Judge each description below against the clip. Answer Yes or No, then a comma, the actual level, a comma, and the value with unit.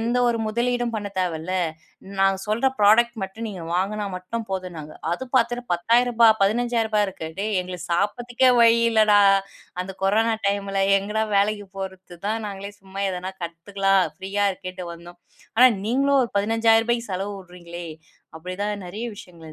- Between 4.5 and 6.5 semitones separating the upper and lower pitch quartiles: No, average, 3.7 semitones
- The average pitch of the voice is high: Yes, high, 200 Hz